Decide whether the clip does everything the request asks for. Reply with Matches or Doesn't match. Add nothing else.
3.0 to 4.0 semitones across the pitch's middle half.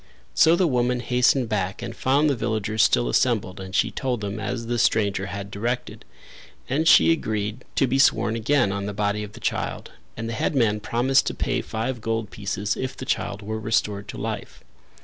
Matches